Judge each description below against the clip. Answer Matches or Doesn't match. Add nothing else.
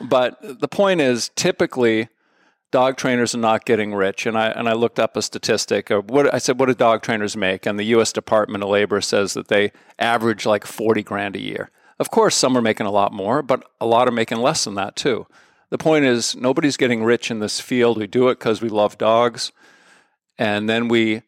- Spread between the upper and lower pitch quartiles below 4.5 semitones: Matches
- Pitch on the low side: Matches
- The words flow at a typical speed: Doesn't match